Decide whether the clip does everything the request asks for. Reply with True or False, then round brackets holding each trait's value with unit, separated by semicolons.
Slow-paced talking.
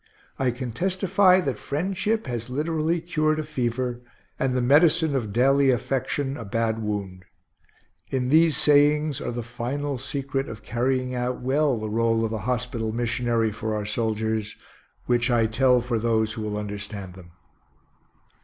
False (155 wpm)